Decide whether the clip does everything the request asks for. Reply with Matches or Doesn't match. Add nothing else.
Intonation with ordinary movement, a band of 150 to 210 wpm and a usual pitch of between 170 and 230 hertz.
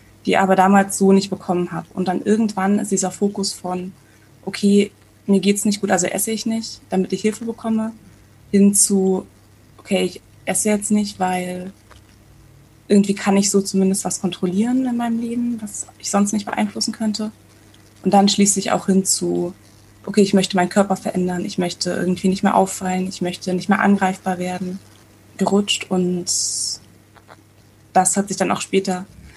Doesn't match